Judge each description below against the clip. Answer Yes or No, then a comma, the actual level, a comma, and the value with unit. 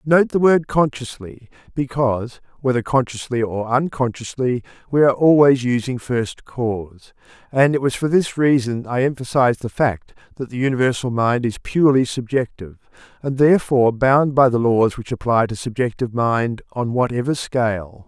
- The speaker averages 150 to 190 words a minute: Yes, average, 155 wpm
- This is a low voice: Yes, low, 125 Hz